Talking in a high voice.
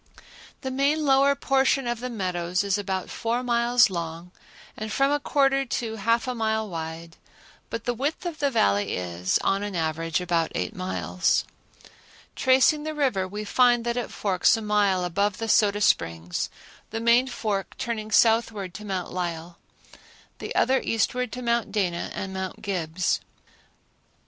Yes: high, 210 Hz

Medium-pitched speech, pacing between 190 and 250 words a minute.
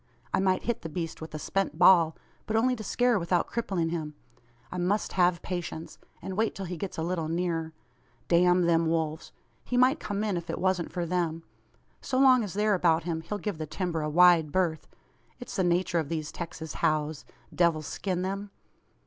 Yes: medium, 175 Hz; average, 200 wpm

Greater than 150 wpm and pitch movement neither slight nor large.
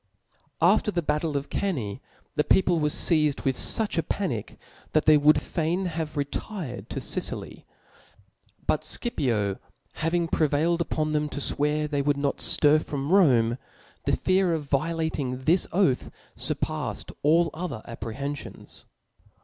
No: average, 140 wpm; average, 3.1 semitones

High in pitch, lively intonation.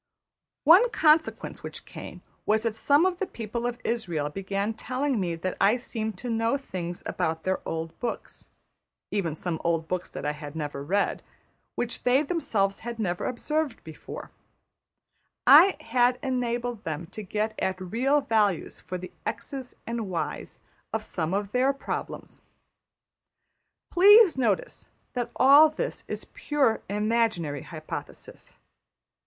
Yes: high, 220 Hz; wide, 6.1 semitones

